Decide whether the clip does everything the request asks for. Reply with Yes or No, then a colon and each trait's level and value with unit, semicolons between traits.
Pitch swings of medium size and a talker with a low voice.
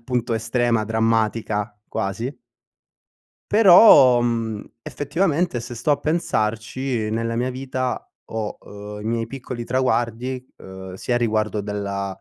Yes: average, 3.1 semitones; low, 115 Hz